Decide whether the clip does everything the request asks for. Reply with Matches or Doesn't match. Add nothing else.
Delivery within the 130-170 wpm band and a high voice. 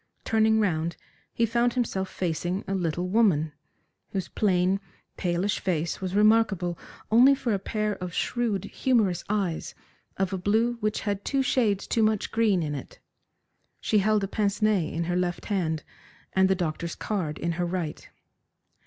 Matches